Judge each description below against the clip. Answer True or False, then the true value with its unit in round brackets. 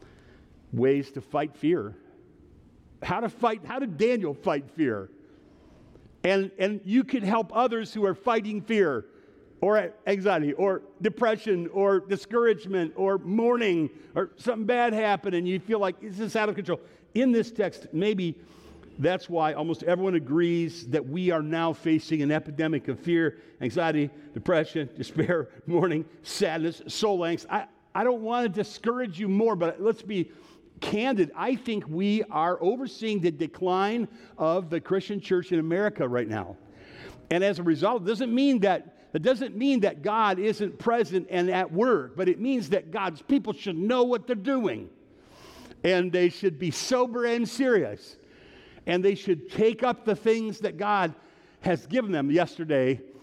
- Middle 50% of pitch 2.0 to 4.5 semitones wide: False (5.0 semitones)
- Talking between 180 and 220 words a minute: False (160 wpm)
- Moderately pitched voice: False (195 Hz)